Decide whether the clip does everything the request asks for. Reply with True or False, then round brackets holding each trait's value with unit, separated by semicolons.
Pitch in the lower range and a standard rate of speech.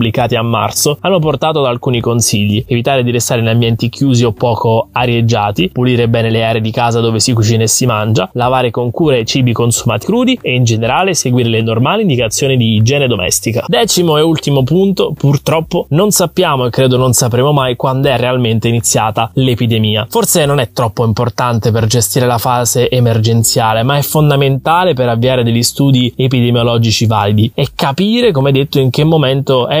False (125 Hz; 180 wpm)